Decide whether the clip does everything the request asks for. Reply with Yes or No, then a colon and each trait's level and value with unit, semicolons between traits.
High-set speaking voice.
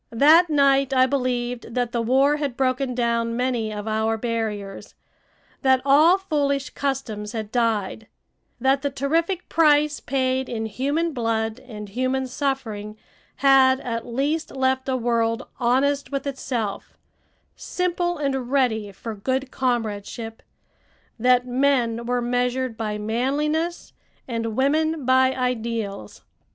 Yes: very high, 255 Hz